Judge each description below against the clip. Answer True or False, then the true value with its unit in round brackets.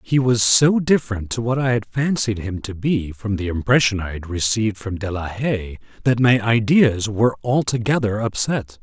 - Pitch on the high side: False (110 Hz)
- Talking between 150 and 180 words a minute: False (190 wpm)